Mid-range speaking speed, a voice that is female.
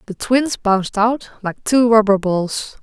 Yes: average, 170 wpm; female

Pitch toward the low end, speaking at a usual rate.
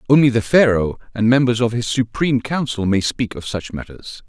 Yes: low, 115 Hz; average, 195 wpm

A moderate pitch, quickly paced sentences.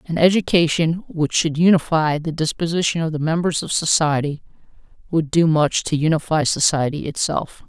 No: medium, 160 Hz; average, 150 wpm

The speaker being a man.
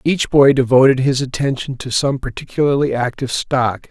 Yes: male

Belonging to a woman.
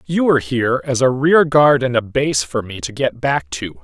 No: male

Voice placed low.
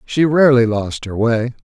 Yes: low, 125 Hz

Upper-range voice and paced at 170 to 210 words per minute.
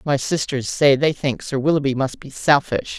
No: medium, 140 Hz; average, 200 wpm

